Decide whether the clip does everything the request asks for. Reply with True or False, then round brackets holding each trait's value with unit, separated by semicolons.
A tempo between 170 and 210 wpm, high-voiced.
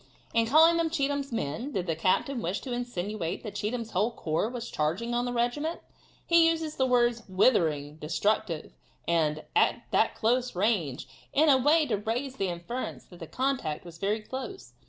True (175 wpm; 230 Hz)